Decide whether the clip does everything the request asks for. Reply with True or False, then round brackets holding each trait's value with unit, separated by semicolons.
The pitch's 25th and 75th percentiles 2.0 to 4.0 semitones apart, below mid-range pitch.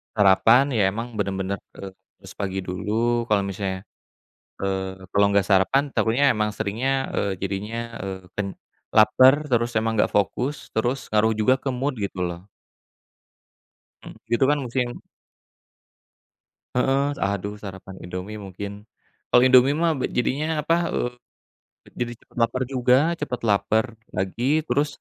False (4.4 semitones; 110 Hz)